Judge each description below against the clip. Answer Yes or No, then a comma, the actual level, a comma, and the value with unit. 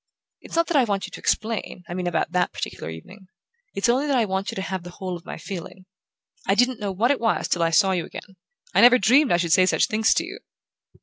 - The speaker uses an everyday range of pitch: Yes, average, 4.8 semitones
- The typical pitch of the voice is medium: No, high, 195 Hz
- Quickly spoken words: Yes, fast, 260 wpm